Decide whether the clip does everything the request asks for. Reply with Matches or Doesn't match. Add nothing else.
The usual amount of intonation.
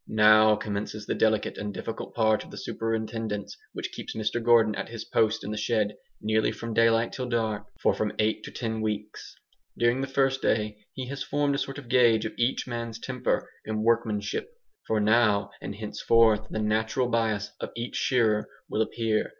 Doesn't match